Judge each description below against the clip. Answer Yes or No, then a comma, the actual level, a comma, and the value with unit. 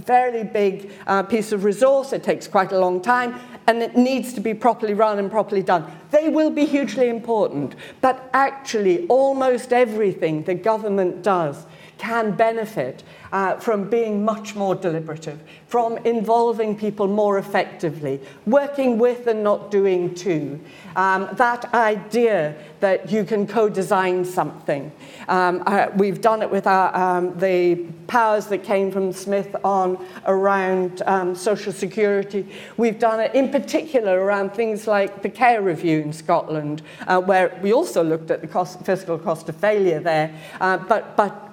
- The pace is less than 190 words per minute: Yes, average, 160 wpm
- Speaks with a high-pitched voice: Yes, high, 200 Hz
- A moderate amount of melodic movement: Yes, average, 3.8 semitones